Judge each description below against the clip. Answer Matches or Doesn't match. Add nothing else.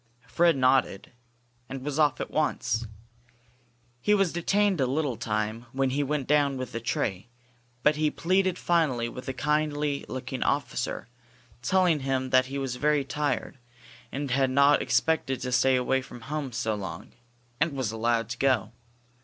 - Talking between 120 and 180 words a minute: Matches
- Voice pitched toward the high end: Doesn't match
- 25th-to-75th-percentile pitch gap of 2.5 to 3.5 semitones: Matches